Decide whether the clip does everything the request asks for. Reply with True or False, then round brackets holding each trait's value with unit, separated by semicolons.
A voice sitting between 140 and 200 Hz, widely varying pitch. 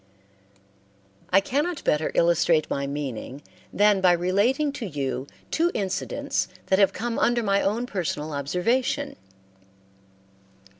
True (190 Hz; 7.6 semitones)